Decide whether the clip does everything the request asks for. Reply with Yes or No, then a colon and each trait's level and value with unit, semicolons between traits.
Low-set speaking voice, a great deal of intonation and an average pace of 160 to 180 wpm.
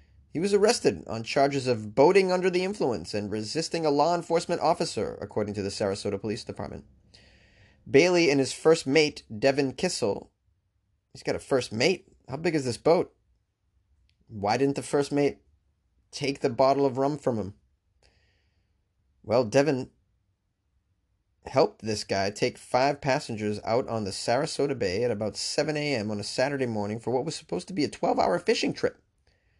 Yes: low, 115 Hz; wide, 6.8 semitones; average, 170 wpm